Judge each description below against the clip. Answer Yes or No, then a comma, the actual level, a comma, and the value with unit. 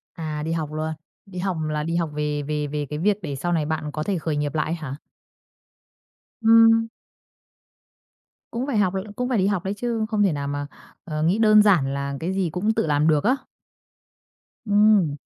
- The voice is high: No, medium, 165 Hz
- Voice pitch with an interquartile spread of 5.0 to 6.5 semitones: Yes, wide, 5.5 semitones